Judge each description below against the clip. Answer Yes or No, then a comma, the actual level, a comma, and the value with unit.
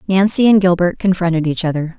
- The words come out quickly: No, average, 180 wpm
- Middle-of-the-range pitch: Yes, medium, 180 Hz